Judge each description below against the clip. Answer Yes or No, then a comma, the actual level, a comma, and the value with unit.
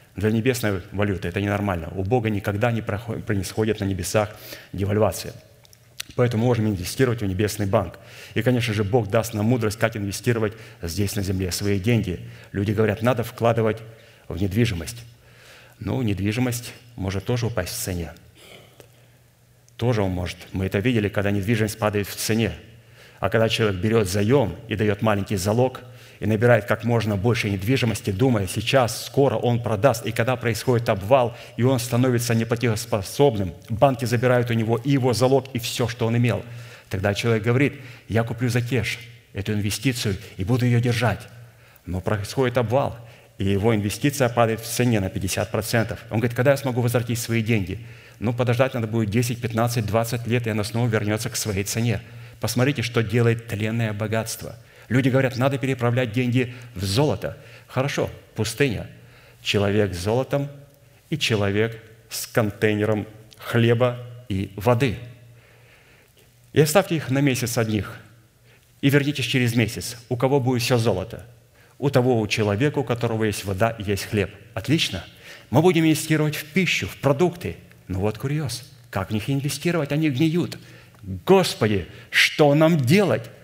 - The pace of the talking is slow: No, average, 155 wpm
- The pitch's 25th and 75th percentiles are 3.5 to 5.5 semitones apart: No, average, 2.8 semitones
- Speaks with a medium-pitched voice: No, low, 115 Hz